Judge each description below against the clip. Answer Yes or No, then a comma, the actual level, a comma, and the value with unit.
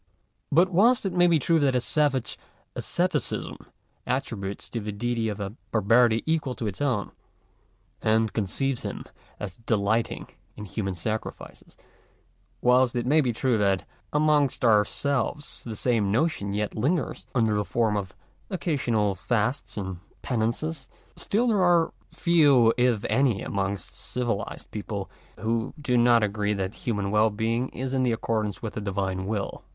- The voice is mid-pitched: No, low, 115 Hz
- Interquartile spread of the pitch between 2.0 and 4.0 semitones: No, average, 4.6 semitones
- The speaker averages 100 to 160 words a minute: Yes, average, 150 wpm